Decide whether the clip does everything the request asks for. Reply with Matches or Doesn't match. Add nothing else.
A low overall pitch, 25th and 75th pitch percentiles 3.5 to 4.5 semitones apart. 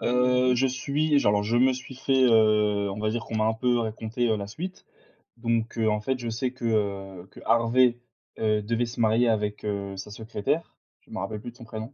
Doesn't match